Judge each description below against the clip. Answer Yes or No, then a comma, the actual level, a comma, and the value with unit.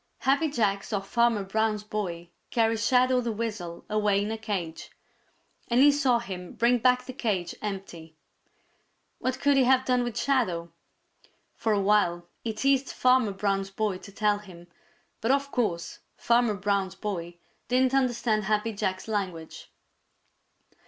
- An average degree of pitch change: Yes, average, 4.2 semitones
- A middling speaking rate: Yes, average, 150 wpm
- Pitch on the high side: Yes, high, 215 Hz